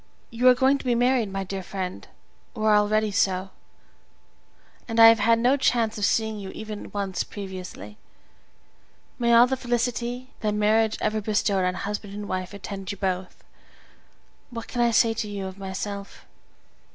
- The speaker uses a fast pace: No, average, 170 wpm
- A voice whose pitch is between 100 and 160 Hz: No, high, 210 Hz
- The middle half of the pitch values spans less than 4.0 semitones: Yes, average, 3.0 semitones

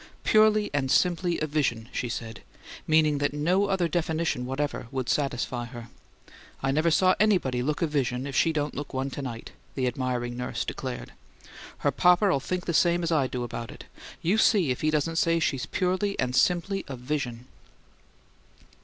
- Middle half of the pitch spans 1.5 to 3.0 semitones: No, average, 5.2 semitones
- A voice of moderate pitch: Yes, medium, 145 Hz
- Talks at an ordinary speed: Yes, average, 175 wpm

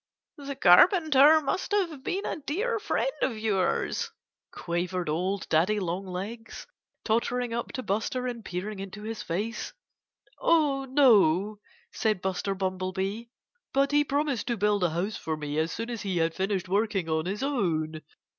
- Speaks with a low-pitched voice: No, high, 210 Hz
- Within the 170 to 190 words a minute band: No, average, 155 wpm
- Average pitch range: No, wide, 6.5 semitones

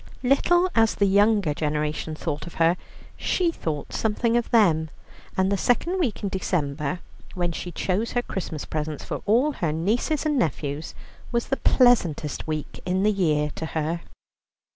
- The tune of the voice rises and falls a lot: Yes, wide, 6.9 semitones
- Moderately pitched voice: Yes, medium, 180 Hz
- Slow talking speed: No, average, 165 wpm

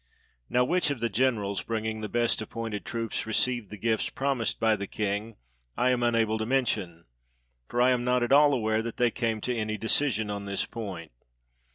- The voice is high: No, low, 115 Hz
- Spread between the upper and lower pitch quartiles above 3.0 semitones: No, narrow, 2.5 semitones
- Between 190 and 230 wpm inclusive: Yes, average, 195 wpm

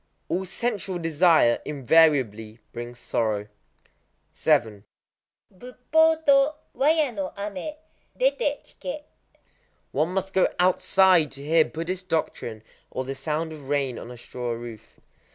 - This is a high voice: No, medium, 165 Hz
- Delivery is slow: Yes, slow, 120 wpm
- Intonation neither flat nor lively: No, wide, 7.9 semitones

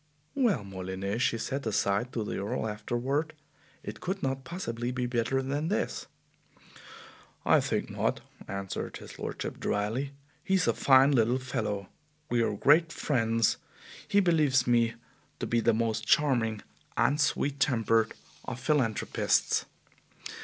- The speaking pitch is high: No, low, 120 Hz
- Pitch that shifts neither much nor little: Yes, average, 4.2 semitones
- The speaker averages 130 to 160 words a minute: Yes, average, 140 wpm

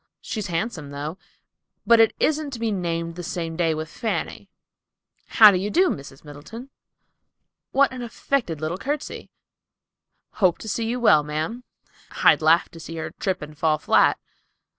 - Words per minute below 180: Yes, average, 145 wpm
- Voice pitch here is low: No, medium, 180 Hz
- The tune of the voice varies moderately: No, wide, 6.6 semitones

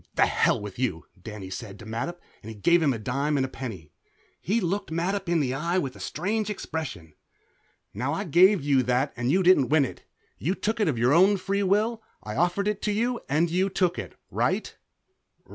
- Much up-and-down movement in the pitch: Yes, wide, 7.4 semitones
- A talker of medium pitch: Yes, medium, 160 Hz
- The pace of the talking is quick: Yes, fast, 210 wpm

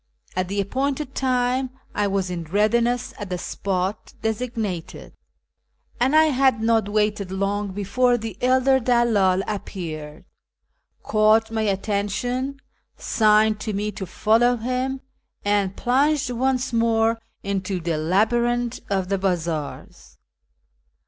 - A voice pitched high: Yes, high, 215 Hz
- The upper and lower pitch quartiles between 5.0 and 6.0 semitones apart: No, average, 4.0 semitones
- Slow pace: Yes, slow, 120 wpm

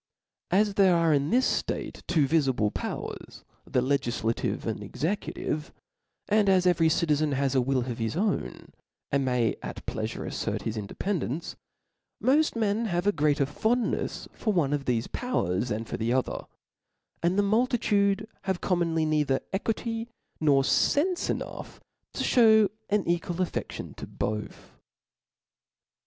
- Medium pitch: Yes, medium, 165 Hz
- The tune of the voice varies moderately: No, wide, 7.2 semitones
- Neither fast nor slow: Yes, average, 145 wpm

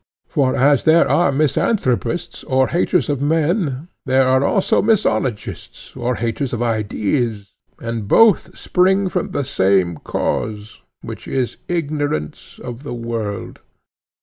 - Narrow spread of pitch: No, wide, 5.4 semitones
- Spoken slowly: Yes, slow, 125 wpm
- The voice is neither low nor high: No, low, 130 Hz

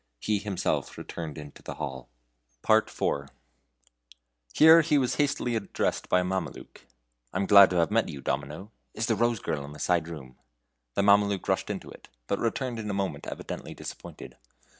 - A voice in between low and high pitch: No, low, 100 Hz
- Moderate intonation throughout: No, wide, 5.9 semitones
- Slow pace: No, average, 170 wpm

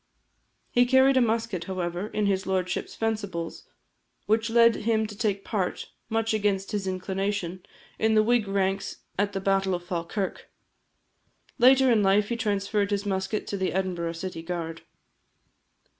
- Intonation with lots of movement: No, average, 2.7 semitones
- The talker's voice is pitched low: No, high, 200 Hz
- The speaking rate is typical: Yes, average, 150 wpm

